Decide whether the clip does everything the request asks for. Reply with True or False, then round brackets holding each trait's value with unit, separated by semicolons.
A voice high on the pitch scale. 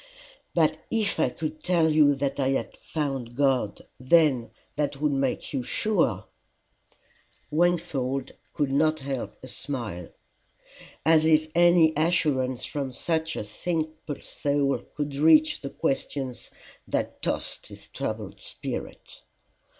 False (145 Hz)